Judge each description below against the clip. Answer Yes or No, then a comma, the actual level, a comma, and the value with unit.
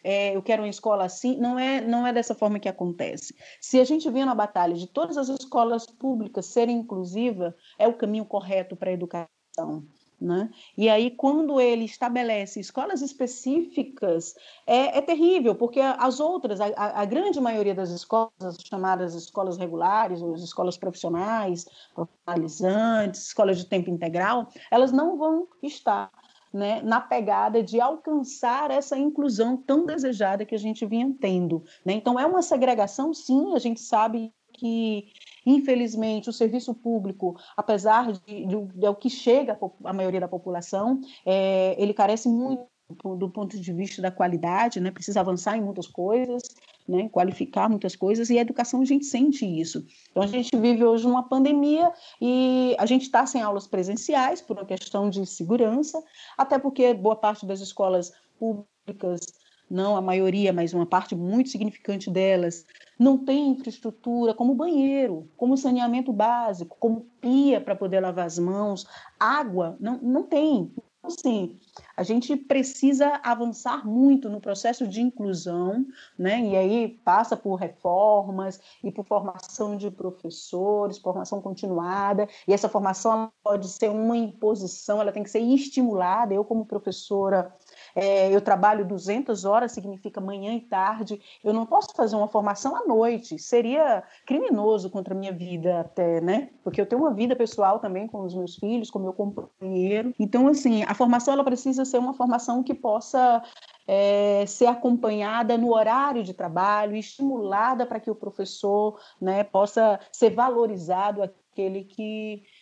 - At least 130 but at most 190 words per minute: Yes, average, 160 wpm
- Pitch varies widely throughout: No, average, 4.4 semitones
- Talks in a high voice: Yes, high, 220 Hz